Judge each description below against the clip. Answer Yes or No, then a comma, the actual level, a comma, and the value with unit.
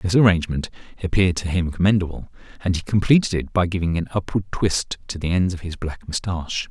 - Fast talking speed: No, average, 195 wpm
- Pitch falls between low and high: No, very low, 90 Hz